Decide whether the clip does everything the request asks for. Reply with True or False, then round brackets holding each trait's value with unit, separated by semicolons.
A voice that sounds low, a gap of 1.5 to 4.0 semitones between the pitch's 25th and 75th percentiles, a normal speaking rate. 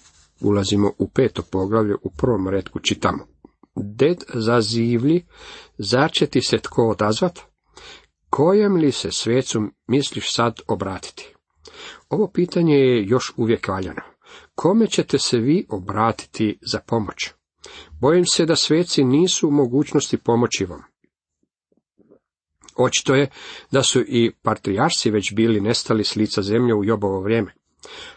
False (120 Hz; 5.6 semitones; 130 wpm)